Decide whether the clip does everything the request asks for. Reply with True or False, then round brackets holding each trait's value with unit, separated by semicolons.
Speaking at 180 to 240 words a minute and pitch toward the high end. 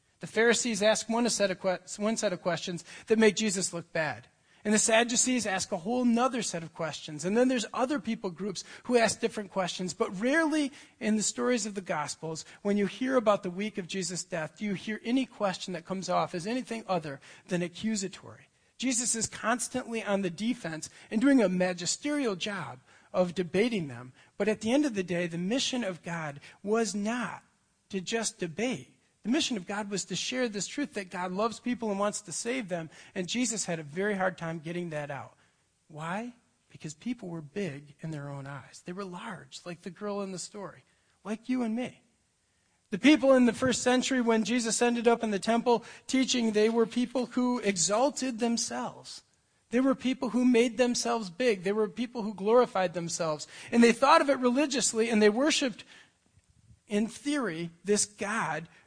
True (195 wpm; 210 Hz)